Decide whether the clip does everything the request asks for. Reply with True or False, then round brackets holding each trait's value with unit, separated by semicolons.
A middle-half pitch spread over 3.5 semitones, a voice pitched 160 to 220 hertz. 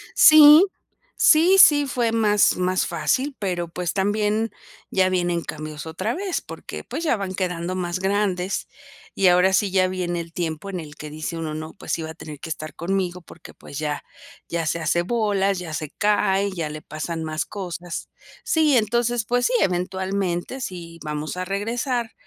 True (4.0 semitones; 185 Hz)